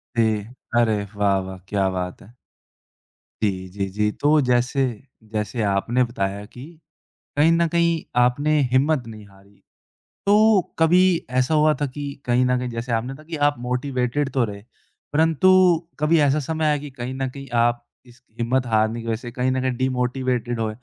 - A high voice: No, low, 125 Hz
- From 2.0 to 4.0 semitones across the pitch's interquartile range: No, average, 4.8 semitones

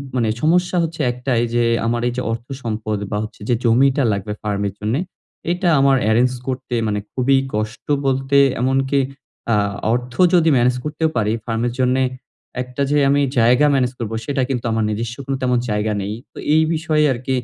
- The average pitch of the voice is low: Yes, low, 125 Hz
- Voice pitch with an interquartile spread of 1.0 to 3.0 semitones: No, average, 3.4 semitones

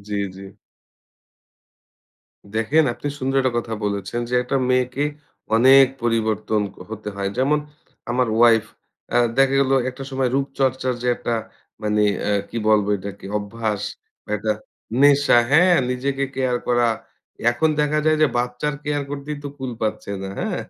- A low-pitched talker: Yes, low, 125 Hz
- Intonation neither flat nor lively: Yes, average, 3.7 semitones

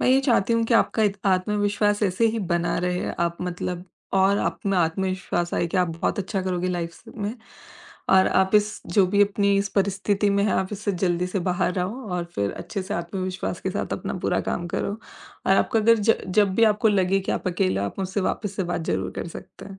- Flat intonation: Yes, narrow, 2.3 semitones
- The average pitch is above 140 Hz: Yes, high, 190 Hz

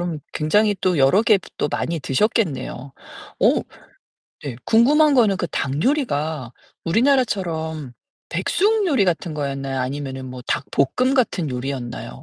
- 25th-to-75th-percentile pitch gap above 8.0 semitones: Yes, wide, 8.5 semitones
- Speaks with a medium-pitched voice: Yes, medium, 160 Hz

